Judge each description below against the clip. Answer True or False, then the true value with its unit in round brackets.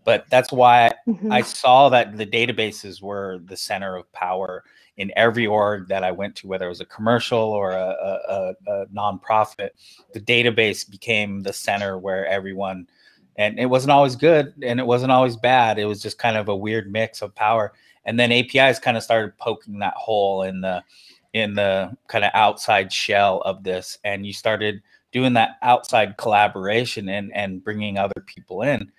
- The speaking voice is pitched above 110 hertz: False (105 Hz)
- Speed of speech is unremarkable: True (185 wpm)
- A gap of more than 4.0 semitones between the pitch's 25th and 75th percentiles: False (3.4 semitones)